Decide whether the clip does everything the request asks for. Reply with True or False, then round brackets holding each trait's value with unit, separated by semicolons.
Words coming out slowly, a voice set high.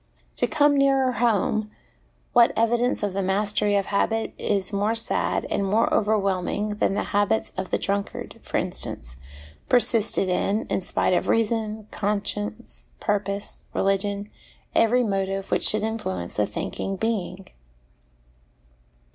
True (130 wpm; 205 Hz)